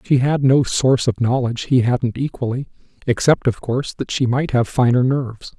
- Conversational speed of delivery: Yes, average, 185 wpm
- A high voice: No, low, 125 Hz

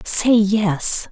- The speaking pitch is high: Yes, high, 205 Hz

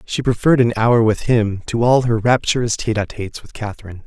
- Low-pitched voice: Yes, low, 115 Hz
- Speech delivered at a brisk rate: Yes, fast, 220 wpm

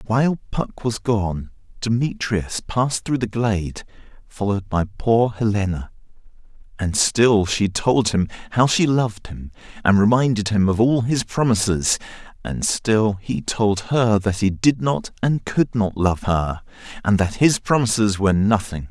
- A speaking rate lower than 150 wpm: No, average, 155 wpm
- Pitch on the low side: Yes, low, 110 Hz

